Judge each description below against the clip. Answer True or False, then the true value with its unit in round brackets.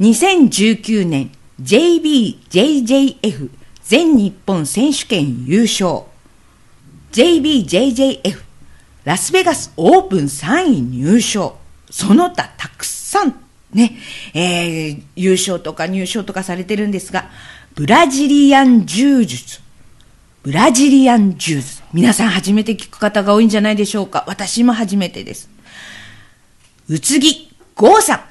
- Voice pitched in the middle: False (215 Hz)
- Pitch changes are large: True (6.9 semitones)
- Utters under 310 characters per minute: True (235 characters per minute)